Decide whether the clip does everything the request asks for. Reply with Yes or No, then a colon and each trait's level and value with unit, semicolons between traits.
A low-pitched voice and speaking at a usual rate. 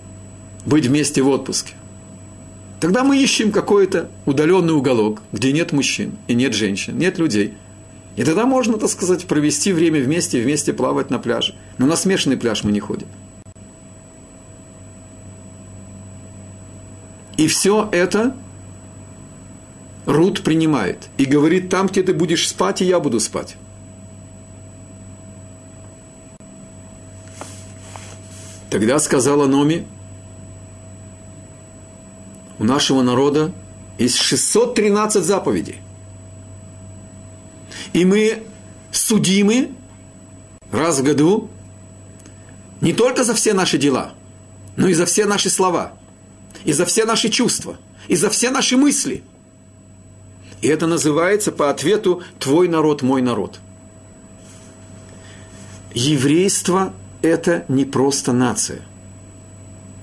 No: low, 105 Hz; slow, 105 wpm